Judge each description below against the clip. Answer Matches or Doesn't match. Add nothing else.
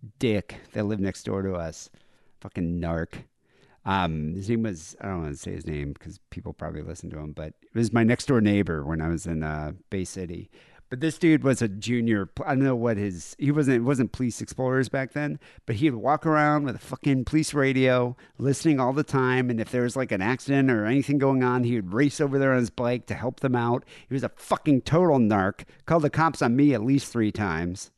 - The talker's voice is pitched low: Matches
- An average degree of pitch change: Doesn't match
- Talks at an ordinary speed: Doesn't match